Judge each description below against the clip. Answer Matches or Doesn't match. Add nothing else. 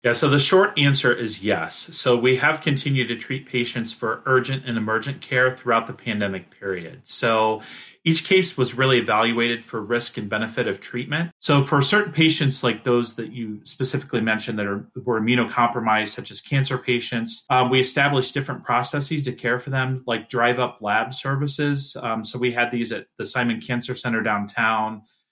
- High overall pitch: Doesn't match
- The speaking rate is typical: Matches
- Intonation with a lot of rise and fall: Doesn't match